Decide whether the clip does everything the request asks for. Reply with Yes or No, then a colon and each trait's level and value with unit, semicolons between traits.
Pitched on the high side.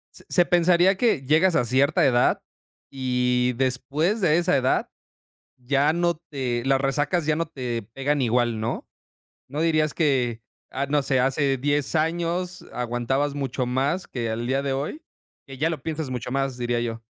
No: low, 135 Hz